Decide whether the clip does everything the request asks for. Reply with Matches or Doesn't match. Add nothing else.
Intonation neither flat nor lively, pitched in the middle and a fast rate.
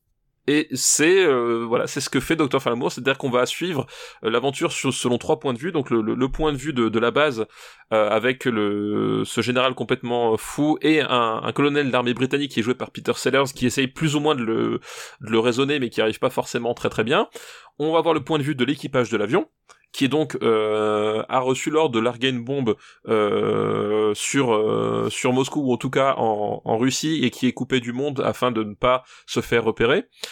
Doesn't match